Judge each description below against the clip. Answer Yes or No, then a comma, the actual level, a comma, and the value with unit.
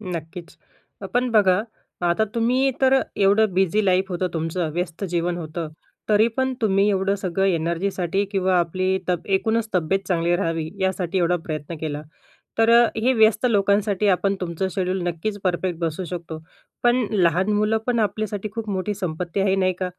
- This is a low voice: No, high, 190 Hz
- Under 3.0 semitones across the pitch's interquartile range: No, average, 3.3 semitones